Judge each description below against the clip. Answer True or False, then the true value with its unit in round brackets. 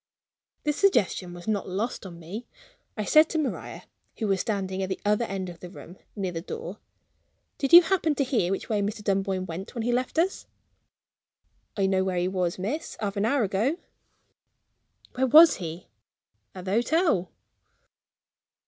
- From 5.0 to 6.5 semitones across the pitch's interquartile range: True (5.5 semitones)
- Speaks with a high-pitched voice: True (205 Hz)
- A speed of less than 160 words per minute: False (175 wpm)